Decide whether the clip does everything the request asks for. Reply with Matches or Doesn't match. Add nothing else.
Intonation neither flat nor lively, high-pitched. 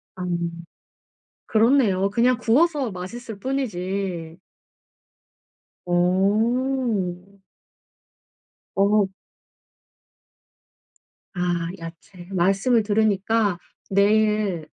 Matches